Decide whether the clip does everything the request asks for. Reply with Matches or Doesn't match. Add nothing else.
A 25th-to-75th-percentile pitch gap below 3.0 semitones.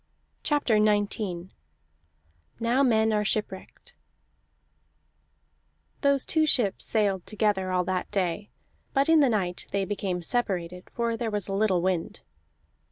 Doesn't match